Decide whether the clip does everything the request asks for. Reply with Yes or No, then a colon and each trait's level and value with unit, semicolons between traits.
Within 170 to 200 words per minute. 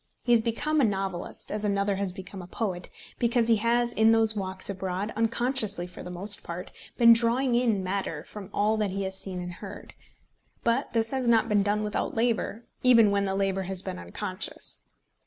Yes: average, 195 wpm